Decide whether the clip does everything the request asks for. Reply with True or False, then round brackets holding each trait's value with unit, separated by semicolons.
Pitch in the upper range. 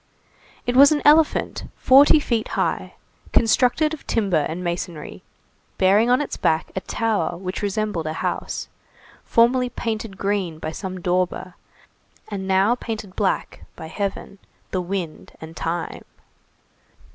True (200 Hz)